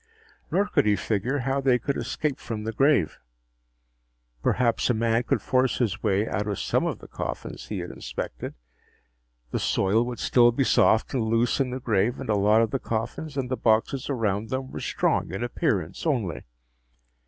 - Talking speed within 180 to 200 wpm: Yes, average, 190 wpm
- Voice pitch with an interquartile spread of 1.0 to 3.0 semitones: No, average, 3.6 semitones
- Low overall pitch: Yes, low, 120 Hz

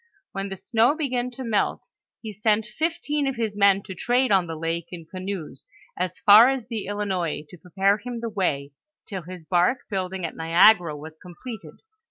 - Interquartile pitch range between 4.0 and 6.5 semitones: Yes, average, 4.7 semitones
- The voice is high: Yes, high, 195 Hz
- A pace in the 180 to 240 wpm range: Yes, average, 185 wpm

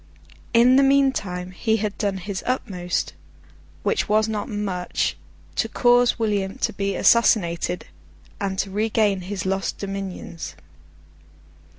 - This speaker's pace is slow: Yes, slow, 120 wpm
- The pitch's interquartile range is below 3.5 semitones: Yes, average, 2.9 semitones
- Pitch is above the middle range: Yes, high, 200 Hz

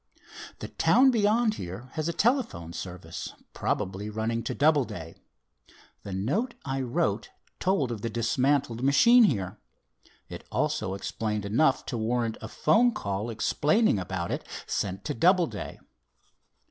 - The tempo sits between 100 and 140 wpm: Yes, slow, 135 wpm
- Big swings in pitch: Yes, wide, 8.3 semitones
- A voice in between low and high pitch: No, low, 120 Hz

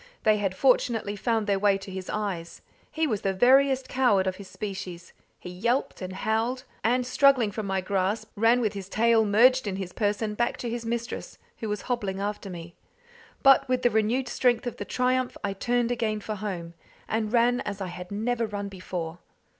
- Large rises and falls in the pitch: No, average, 3.8 semitones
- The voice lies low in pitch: No, high, 215 Hz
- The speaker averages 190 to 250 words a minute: Yes, average, 195 wpm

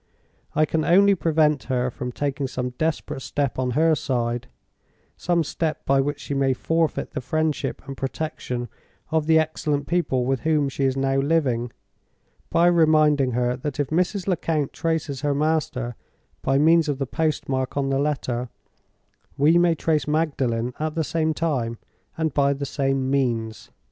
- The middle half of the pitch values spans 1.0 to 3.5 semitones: Yes, average, 3.2 semitones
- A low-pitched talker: No, medium, 145 Hz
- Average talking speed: Yes, average, 160 wpm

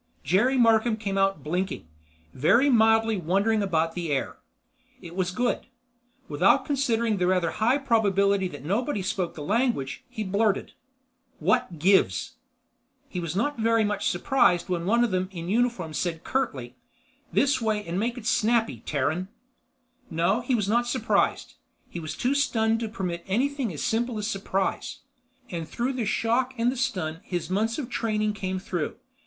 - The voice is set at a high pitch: Yes, high, 205 Hz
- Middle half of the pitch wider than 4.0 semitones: Yes, average, 4.8 semitones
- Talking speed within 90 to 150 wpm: No, average, 160 wpm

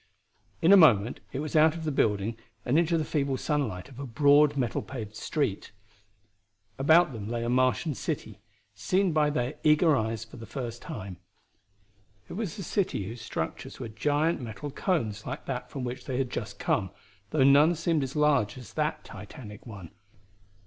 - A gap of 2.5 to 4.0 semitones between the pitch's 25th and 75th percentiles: No, average, 5.3 semitones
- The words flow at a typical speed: Yes, average, 180 wpm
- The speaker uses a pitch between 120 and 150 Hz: Yes, low, 135 Hz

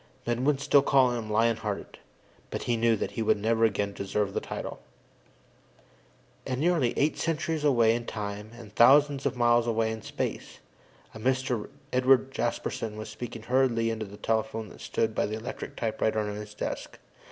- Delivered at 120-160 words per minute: No, average, 175 wpm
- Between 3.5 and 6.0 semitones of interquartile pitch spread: No, average, 3.0 semitones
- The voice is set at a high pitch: No, low, 115 Hz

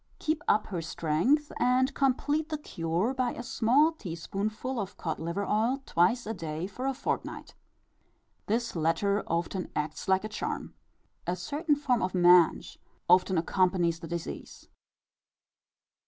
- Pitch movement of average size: No, wide, 6.8 semitones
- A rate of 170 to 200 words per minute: No, average, 145 wpm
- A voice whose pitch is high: Yes, high, 200 Hz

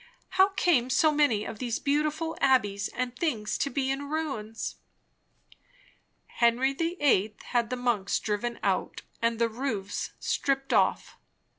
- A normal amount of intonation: Yes, average, 4.5 semitones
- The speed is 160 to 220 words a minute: No, average, 140 wpm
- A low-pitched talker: No, very high, 255 Hz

